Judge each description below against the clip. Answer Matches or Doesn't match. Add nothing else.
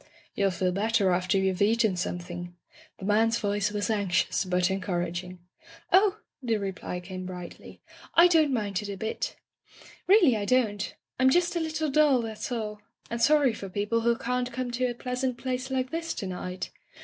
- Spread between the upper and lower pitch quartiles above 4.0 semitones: Matches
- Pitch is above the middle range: Matches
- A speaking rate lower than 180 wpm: Doesn't match